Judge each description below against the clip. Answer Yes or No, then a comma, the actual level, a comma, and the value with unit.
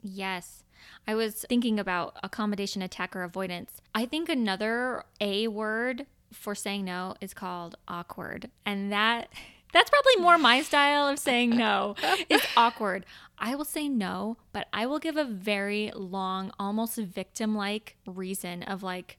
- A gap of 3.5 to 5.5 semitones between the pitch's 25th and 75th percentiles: Yes, average, 4.0 semitones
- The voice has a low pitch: No, high, 215 Hz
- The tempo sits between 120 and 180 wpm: Yes, average, 150 wpm